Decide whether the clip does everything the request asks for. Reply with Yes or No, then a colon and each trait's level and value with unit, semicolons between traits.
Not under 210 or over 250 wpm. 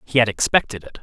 Yes: fast, 235 wpm